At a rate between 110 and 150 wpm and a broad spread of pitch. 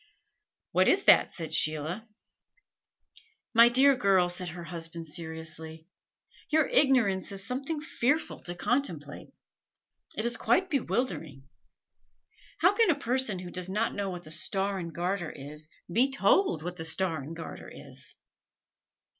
Yes: average, 140 wpm; wide, 7.4 semitones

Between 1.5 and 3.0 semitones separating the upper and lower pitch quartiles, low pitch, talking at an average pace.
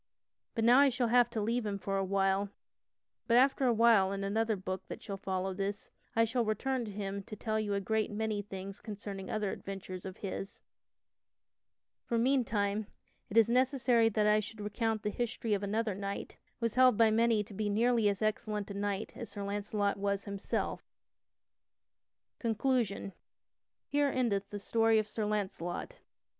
No: narrow, 2.5 semitones; high, 210 Hz; average, 175 wpm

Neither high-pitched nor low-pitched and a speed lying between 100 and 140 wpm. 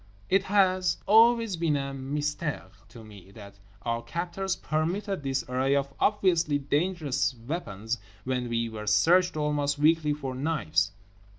Yes: medium, 145 Hz; slow, 135 wpm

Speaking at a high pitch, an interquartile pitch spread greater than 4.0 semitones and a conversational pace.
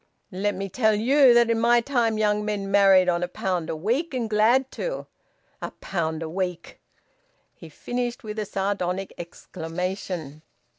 Yes: high, 205 Hz; average, 4.5 semitones; average, 160 wpm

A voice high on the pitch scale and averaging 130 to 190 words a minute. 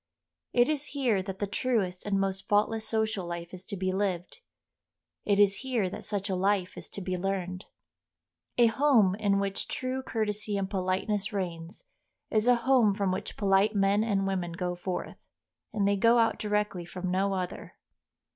Yes: high, 200 Hz; average, 175 wpm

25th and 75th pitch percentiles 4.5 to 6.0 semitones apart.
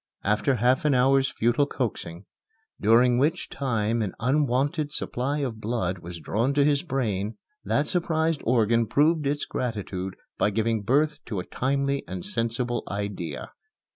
Yes: average, 4.9 semitones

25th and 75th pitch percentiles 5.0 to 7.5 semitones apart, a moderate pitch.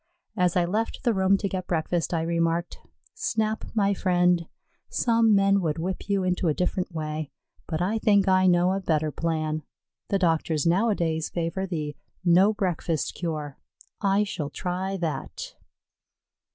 No: average, 3.1 semitones; medium, 180 Hz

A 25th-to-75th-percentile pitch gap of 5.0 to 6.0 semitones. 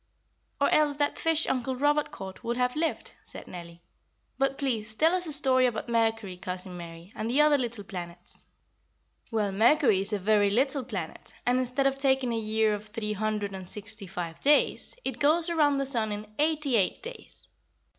Yes: average, 5.3 semitones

